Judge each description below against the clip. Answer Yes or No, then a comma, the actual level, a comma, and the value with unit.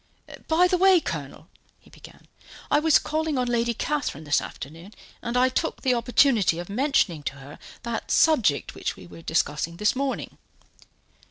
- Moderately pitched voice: No, high, 240 Hz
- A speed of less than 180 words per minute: Yes, average, 165 wpm